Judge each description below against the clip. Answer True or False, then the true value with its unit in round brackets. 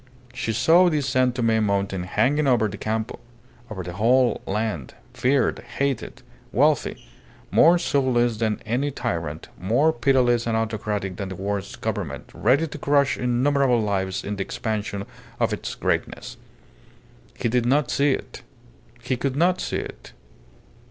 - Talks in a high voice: False (120 Hz)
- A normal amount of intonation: True (4.8 semitones)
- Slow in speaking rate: False (145 wpm)